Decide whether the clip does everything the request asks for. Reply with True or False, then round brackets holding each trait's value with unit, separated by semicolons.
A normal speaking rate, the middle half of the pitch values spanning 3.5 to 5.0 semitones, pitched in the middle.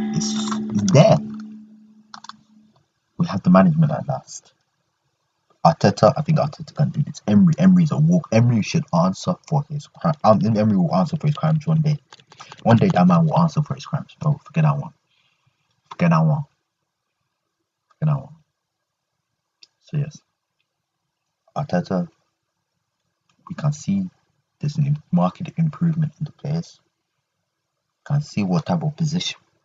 False (150 wpm; 2.8 semitones; 160 Hz)